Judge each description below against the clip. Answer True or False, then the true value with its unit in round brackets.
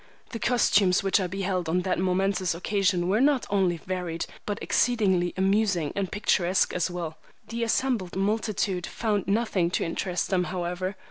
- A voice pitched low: False (190 Hz)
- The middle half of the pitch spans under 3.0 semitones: True (2.5 semitones)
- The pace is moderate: True (155 wpm)